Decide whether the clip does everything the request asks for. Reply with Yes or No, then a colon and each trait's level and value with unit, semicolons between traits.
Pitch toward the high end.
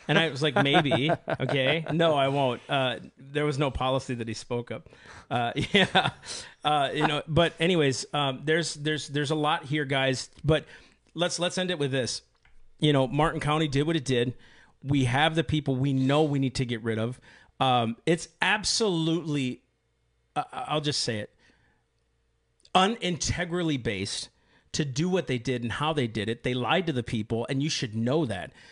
No: medium, 140 Hz